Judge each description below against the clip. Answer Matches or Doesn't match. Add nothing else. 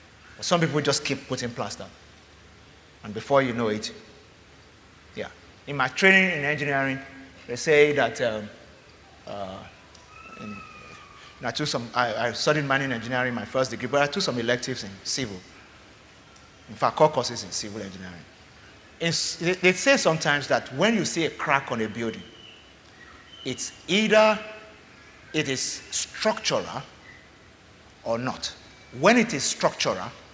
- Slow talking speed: Doesn't match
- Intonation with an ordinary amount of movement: Doesn't match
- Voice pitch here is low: Matches